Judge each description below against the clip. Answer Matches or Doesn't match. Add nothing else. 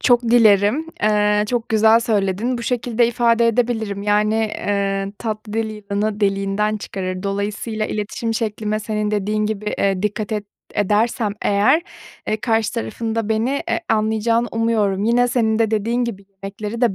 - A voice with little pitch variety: Matches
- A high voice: Matches